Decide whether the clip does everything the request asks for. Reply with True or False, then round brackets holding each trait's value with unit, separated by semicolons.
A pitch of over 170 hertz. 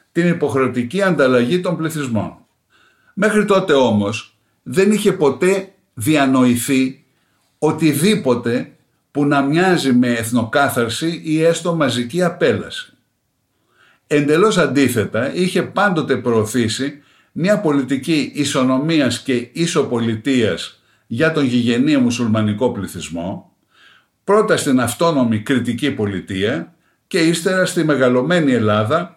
False (140 Hz)